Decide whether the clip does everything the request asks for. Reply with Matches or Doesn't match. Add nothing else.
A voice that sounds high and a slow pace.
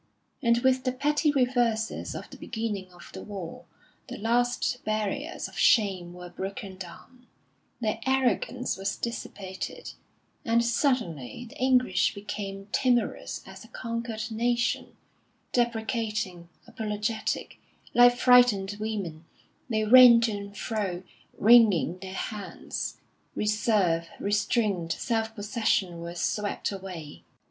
Matches